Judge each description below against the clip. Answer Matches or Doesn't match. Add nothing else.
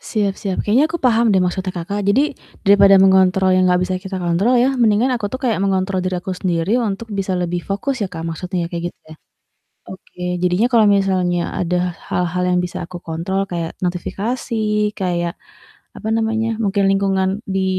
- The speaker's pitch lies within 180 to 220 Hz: Matches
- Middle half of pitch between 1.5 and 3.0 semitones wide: Matches